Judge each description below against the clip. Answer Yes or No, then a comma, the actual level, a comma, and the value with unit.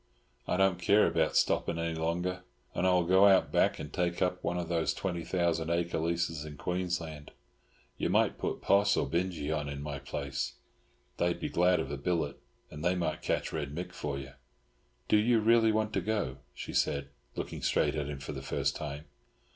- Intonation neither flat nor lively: Yes, average, 3.5 semitones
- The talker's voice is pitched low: Yes, very low, 85 Hz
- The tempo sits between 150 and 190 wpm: No, average, 200 wpm